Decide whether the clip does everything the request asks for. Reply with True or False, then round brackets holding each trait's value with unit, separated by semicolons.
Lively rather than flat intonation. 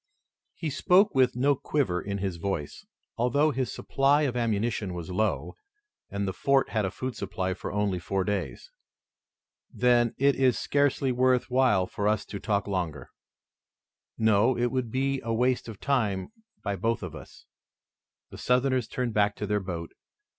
False (4.6 semitones)